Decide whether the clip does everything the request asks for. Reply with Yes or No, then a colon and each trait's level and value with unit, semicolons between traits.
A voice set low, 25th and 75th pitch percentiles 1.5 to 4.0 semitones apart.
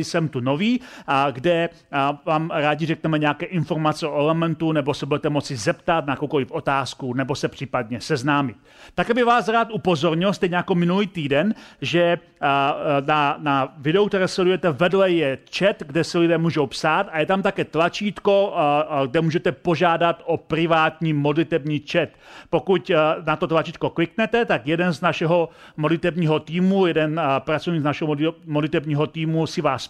No: medium, 165 Hz; average, 2.8 semitones